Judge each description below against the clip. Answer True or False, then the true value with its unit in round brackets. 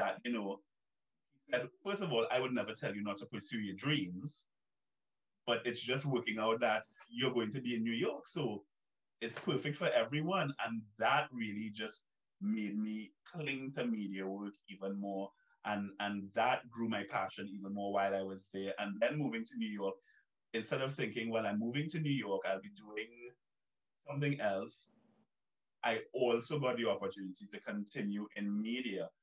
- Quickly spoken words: False (180 wpm)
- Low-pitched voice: True (115 Hz)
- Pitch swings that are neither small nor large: True (4.2 semitones)